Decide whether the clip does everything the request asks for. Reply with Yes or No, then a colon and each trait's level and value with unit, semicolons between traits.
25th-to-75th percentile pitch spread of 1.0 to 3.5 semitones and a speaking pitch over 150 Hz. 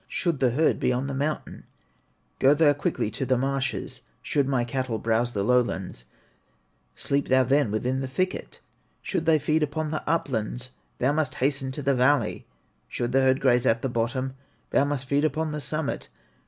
No: average, 2.8 semitones; low, 135 Hz